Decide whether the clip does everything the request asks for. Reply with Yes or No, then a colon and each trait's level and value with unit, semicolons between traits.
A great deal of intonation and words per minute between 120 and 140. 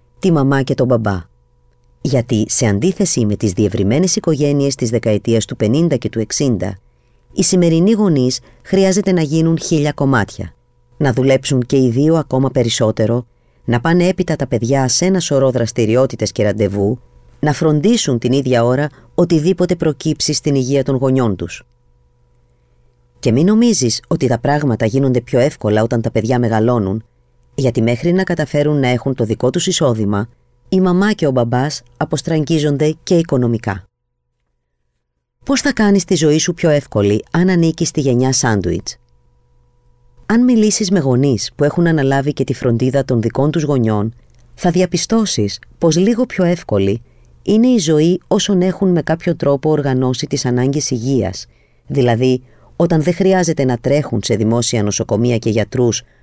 No: wide, 6.5 semitones; average, 155 wpm